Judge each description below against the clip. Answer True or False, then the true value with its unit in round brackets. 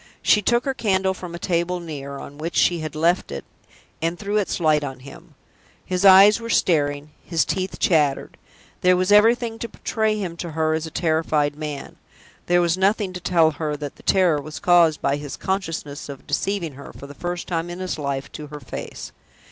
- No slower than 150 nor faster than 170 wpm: False (205 wpm)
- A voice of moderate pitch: True (170 Hz)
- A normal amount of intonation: True (4.0 semitones)